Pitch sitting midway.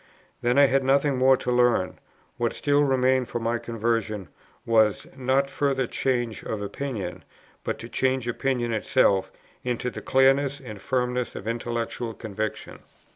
No: low, 125 Hz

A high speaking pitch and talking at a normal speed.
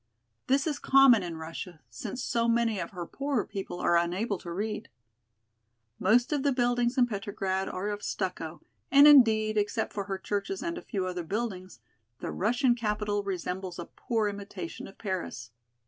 Yes: high, 210 Hz; average, 170 wpm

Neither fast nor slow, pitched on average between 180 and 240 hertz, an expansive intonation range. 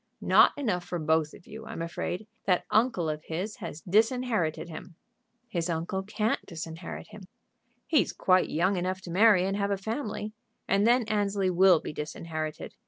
No: average, 170 wpm; medium, 185 Hz; average, 4.2 semitones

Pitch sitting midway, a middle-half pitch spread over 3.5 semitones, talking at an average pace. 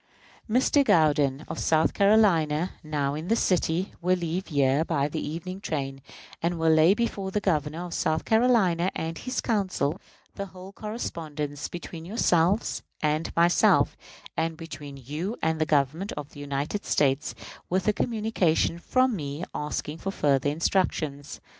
Yes: medium, 165 Hz; average, 4.3 semitones; average, 145 wpm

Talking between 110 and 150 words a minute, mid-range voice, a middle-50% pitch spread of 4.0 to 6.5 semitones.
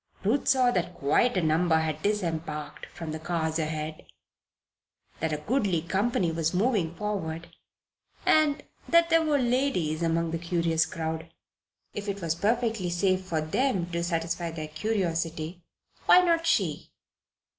Yes: average, 145 wpm; medium, 170 Hz; average, 4.8 semitones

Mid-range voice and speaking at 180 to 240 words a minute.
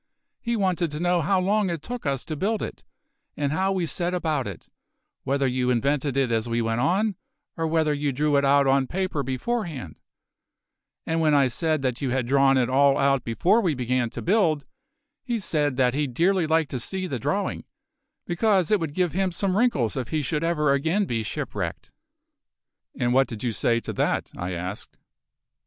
Yes: medium, 150 Hz; average, 195 wpm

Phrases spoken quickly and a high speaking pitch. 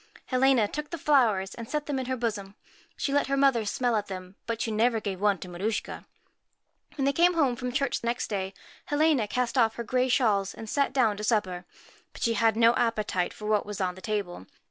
Yes: fast, 220 wpm; high, 230 Hz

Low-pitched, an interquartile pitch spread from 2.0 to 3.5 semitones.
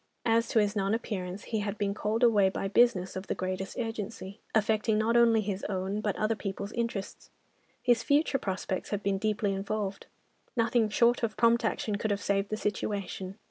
No: high, 210 Hz; narrow, 2.5 semitones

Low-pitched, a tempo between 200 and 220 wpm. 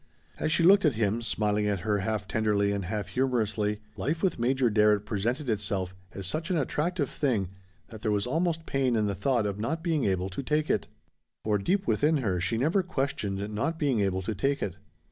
Yes: low, 110 Hz; fast, 205 wpm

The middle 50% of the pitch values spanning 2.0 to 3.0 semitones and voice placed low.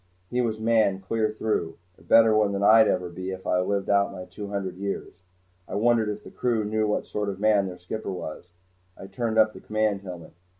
Yes: narrow, 2.5 semitones; low, 105 Hz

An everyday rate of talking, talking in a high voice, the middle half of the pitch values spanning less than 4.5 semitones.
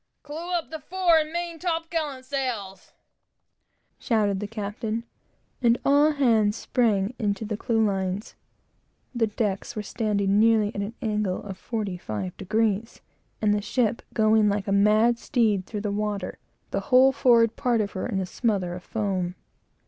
Yes: average, 160 wpm; high, 215 Hz; average, 3.6 semitones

